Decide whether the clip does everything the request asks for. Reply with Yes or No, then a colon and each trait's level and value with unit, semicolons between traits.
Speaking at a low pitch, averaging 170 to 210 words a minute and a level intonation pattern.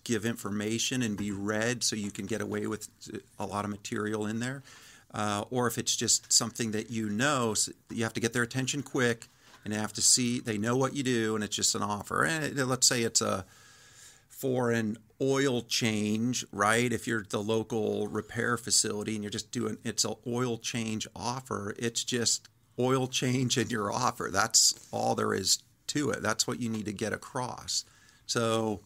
Yes: low, 115 Hz; average, 200 wpm; narrow, 2.3 semitones